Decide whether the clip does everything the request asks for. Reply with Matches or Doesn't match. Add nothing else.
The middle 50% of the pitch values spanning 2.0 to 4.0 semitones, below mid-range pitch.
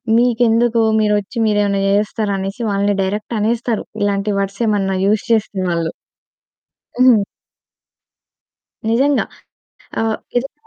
Doesn't match